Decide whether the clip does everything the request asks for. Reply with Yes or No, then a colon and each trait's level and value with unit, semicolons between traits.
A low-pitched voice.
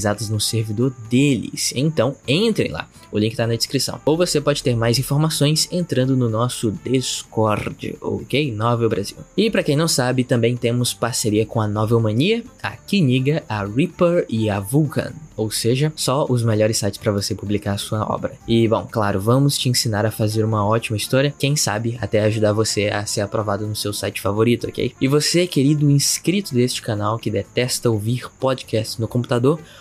Yes: low, 115 Hz